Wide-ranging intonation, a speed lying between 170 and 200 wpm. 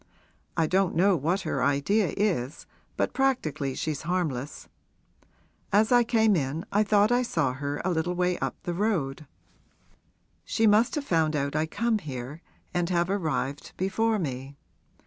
No: wide, 6.3 semitones; average, 155 wpm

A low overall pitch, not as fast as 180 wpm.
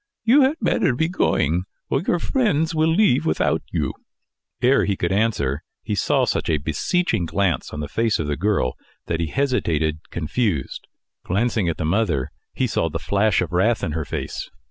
No: low, 100 Hz; average, 185 wpm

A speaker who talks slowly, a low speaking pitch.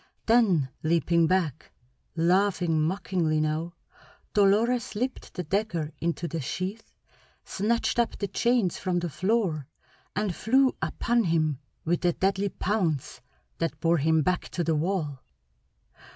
No: slow, 130 wpm; medium, 180 Hz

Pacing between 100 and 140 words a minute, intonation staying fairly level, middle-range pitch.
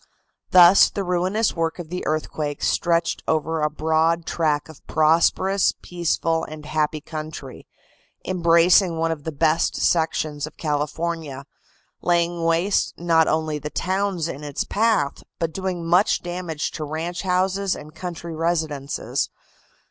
Yes: slow, 135 wpm; narrow, 2.2 semitones; medium, 165 Hz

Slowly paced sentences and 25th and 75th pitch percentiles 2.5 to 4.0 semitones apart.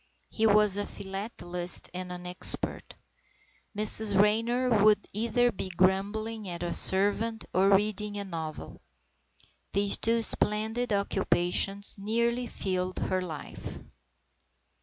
Yes: slow, 115 wpm; average, 2.8 semitones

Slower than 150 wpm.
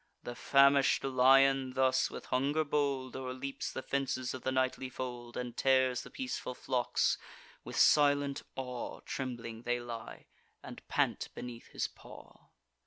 Yes: average, 140 wpm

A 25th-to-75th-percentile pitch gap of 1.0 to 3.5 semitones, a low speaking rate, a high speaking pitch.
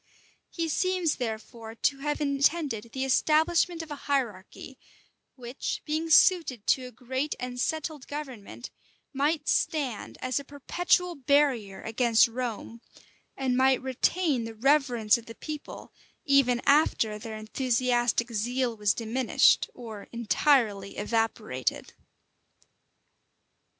No: average, 4.3 semitones; slow, 115 wpm; very high, 255 Hz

